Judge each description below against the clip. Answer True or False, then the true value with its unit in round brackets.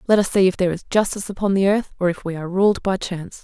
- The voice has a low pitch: False (190 Hz)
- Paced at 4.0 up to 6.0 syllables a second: False (7.2 syllables/s)